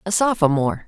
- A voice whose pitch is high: No, medium, 175 Hz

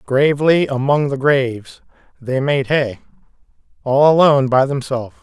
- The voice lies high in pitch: No, low, 135 Hz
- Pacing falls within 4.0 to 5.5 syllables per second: Yes, 4.9 syllables/s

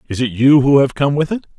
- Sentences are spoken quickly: Yes, fast, 300 wpm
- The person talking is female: No, male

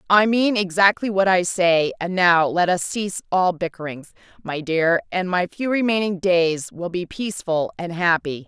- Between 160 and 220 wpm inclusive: Yes, average, 175 wpm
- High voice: No, medium, 180 Hz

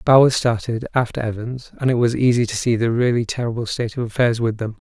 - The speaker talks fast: Yes, fast, 220 wpm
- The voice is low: Yes, low, 120 Hz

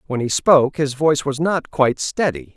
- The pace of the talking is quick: Yes, fast, 210 wpm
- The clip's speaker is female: No, male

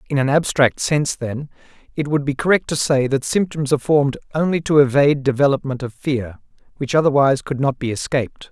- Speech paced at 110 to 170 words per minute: No, average, 190 wpm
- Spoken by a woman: No, male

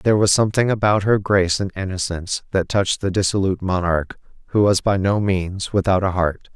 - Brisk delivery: No, average, 190 wpm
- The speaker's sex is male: Yes, male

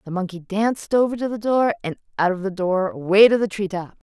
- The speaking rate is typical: No, fast, 250 wpm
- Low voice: No, high, 200 Hz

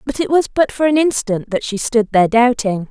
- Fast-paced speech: Yes, fast, 250 wpm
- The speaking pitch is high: Yes, high, 240 Hz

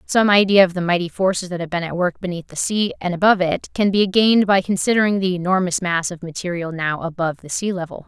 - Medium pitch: Yes, medium, 180 Hz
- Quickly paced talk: Yes, fast, 230 wpm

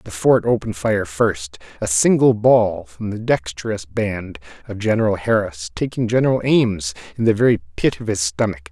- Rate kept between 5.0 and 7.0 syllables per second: No, 4.8 syllables/s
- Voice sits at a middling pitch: No, low, 115 Hz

